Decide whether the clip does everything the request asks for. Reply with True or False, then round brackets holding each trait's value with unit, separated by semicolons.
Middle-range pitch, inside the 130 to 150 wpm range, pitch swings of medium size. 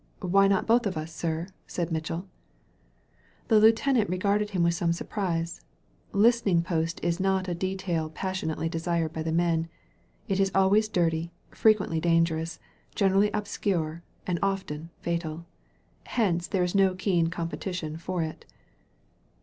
True (175 Hz; 140 wpm; 3.0 semitones)